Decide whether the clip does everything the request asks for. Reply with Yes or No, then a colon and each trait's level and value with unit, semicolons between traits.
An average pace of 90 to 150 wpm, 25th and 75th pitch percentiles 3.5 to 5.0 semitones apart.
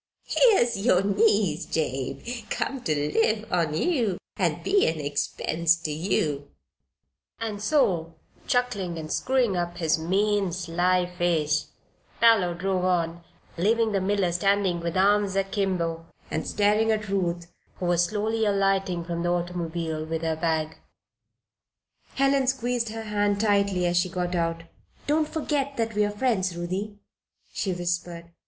Yes: average, 145 wpm; average, 3.8 semitones